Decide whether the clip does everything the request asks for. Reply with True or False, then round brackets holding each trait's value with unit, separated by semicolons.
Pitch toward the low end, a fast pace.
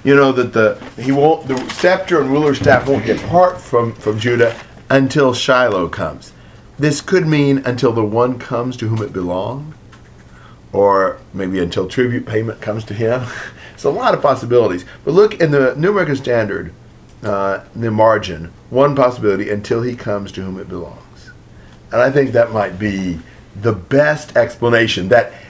False (120 Hz; 165 wpm)